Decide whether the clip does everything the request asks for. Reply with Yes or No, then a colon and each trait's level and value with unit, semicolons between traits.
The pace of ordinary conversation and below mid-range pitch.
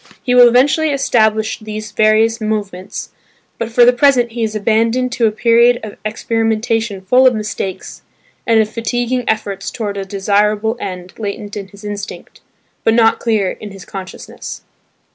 No: average, 160 wpm; high, 220 Hz